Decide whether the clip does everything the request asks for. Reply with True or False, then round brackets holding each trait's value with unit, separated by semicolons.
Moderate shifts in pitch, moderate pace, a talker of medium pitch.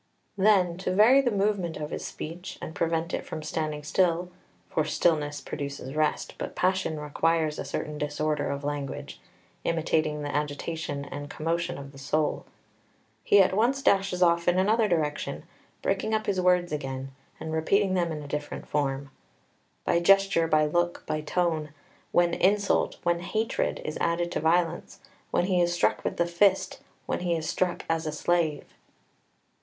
True (3.2 semitones; 170 wpm; 165 Hz)